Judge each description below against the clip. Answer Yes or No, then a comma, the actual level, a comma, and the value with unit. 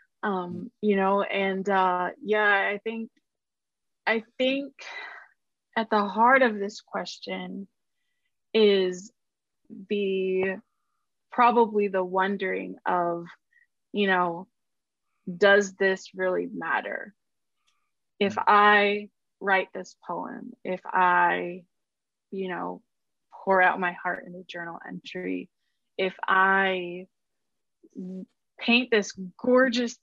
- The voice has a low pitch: No, high, 200 Hz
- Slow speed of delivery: Yes, slow, 100 wpm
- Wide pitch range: No, average, 4.0 semitones